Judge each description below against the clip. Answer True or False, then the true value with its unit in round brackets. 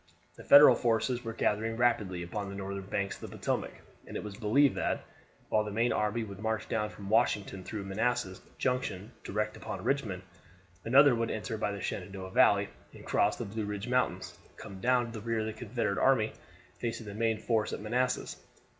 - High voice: False (110 Hz)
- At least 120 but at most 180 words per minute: False (195 wpm)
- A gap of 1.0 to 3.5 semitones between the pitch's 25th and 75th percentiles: True (2.9 semitones)